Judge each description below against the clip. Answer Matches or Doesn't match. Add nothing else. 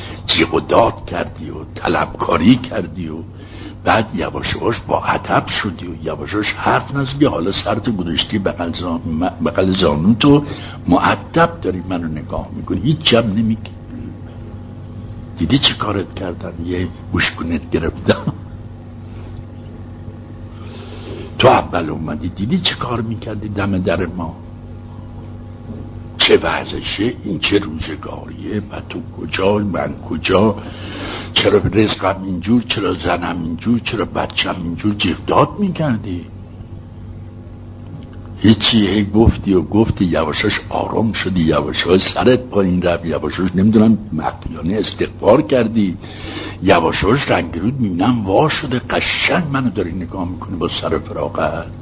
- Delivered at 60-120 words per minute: Matches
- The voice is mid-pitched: Doesn't match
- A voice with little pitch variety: Doesn't match